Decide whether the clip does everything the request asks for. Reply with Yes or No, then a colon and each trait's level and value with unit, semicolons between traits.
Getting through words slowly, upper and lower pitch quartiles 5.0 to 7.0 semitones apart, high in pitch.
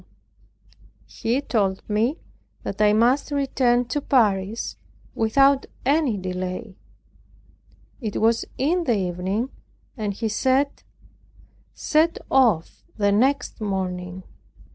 Yes: slow, 100 wpm; average, 5.3 semitones; high, 225 Hz